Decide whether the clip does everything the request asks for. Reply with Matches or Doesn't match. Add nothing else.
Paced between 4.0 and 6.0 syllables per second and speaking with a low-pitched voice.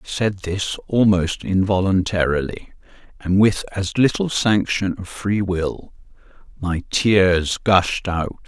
Doesn't match